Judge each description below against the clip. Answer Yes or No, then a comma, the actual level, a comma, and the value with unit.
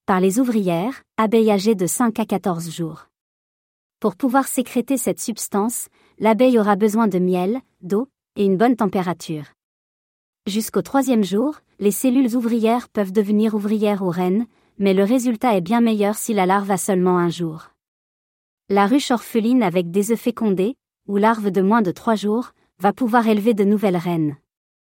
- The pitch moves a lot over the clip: No, average, 3.7 semitones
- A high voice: Yes, high, 210 Hz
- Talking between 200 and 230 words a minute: No, average, 165 wpm